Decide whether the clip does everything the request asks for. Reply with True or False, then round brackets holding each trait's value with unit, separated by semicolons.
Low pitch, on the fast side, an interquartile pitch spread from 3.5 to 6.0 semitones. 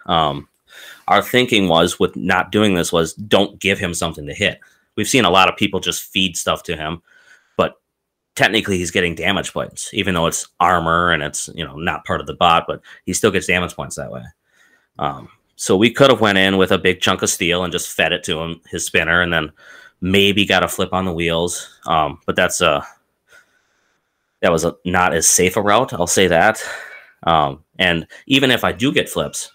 False (90 Hz; 215 wpm; 2.7 semitones)